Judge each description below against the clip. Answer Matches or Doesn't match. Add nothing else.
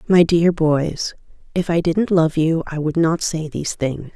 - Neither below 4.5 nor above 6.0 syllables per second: Doesn't match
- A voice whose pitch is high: Doesn't match